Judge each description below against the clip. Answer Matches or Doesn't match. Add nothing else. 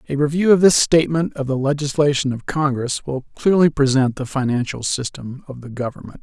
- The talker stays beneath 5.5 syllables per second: Doesn't match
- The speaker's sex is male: Matches